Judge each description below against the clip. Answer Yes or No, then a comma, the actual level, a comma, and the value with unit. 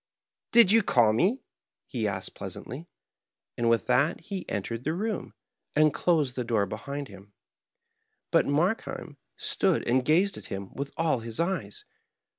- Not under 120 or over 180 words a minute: Yes, average, 160 wpm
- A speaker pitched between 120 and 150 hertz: Yes, medium, 140 Hz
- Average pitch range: No, wide, 7.3 semitones